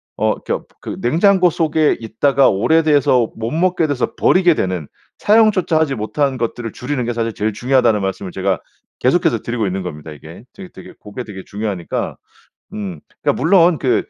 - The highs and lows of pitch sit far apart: Yes, wide, 7.5 semitones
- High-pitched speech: No, low, 120 Hz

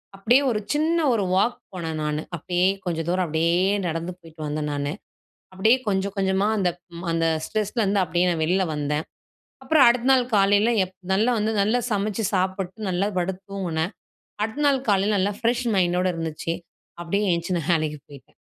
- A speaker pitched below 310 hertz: Yes, high, 190 Hz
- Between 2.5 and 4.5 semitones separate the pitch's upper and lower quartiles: Yes, average, 4.0 semitones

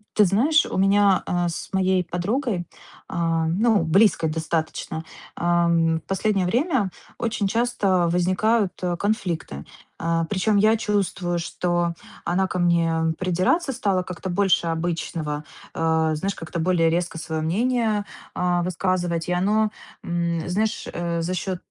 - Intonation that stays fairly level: No, average, 3.3 semitones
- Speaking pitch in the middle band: Yes, medium, 180 Hz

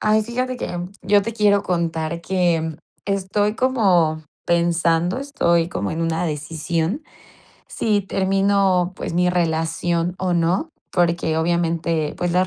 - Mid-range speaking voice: Yes, medium, 175 Hz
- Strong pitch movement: No, average, 3.1 semitones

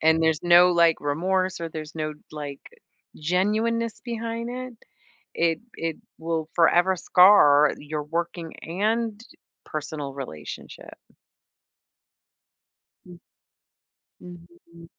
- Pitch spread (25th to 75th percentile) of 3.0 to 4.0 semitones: Yes, average, 3.5 semitones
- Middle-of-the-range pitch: Yes, medium, 170 Hz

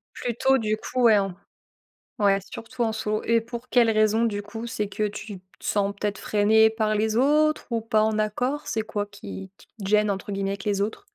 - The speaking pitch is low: No, high, 215 Hz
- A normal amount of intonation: No, narrow, 2.0 semitones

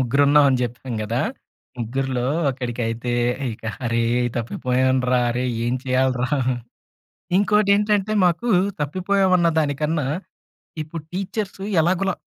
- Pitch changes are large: Yes, wide, 6.8 semitones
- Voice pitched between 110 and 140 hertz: Yes, low, 135 Hz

